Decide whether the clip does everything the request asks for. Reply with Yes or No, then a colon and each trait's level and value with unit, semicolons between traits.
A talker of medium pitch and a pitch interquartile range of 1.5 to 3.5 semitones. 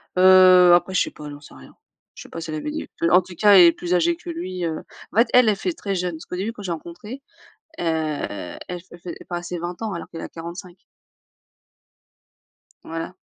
Yes: medium, 180 Hz; average, 2.9 semitones